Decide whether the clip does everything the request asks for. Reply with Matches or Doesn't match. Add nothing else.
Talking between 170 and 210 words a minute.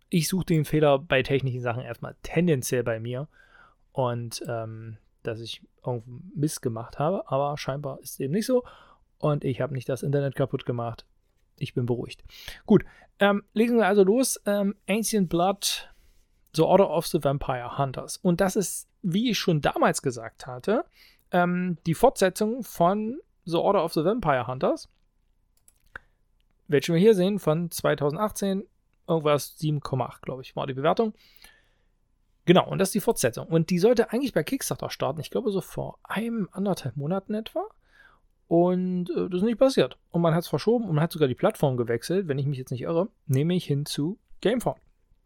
Matches